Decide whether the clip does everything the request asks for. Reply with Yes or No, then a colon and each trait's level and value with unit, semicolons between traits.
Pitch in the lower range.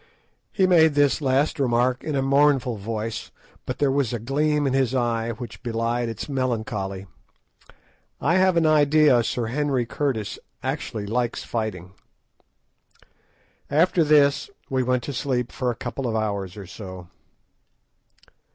Yes: low, 125 Hz